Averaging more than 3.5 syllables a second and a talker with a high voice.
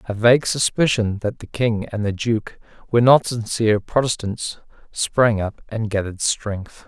No: 4.6 syllables/s; low, 110 Hz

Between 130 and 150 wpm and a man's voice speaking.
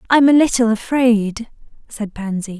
No: average, 140 wpm; female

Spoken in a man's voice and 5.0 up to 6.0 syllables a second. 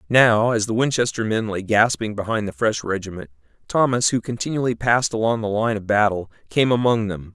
Yes: male; 5.6 syllables/s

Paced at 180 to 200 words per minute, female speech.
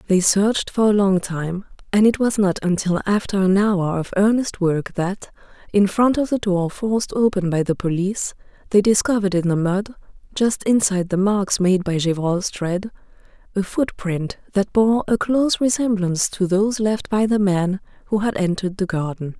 Yes: average, 185 wpm; female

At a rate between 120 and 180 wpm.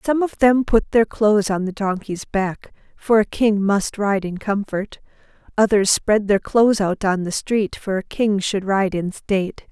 No: average, 200 wpm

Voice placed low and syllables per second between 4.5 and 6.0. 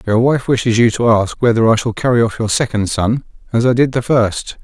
Yes: low, 115 Hz; 5.5 syllables/s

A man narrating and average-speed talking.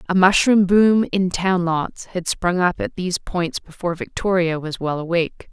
No: female; average, 185 wpm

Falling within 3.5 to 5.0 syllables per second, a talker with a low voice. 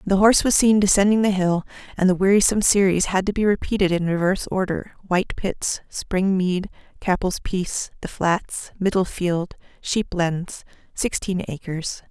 No: 4.9 syllables/s; high, 190 Hz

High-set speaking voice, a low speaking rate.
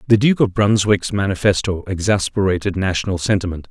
No: low, 100 Hz; slow, 130 wpm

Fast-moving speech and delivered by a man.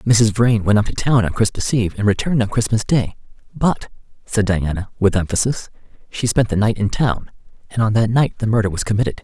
Yes: fast, 215 wpm; male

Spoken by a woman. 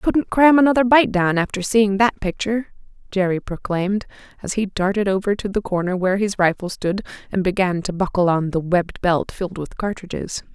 Yes: female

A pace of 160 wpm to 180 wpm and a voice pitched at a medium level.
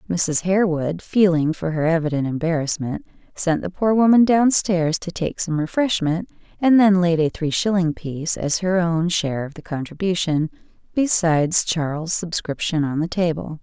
Yes: average, 165 wpm; medium, 170 Hz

